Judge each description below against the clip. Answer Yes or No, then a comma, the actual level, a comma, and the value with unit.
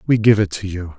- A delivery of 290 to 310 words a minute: Yes, fast, 305 wpm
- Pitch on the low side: Yes, low, 100 Hz